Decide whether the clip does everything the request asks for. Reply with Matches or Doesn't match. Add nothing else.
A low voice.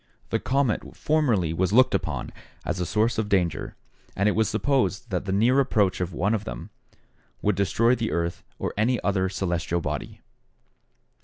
Matches